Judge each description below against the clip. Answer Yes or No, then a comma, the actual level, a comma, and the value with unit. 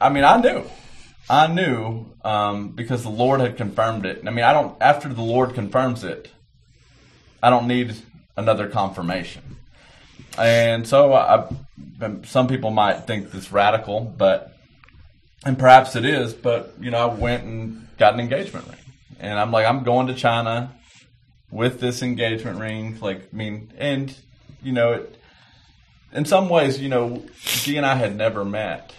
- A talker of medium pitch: No, low, 120 Hz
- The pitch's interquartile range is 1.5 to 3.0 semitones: Yes, average, 2.7 semitones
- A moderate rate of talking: Yes, average, 170 wpm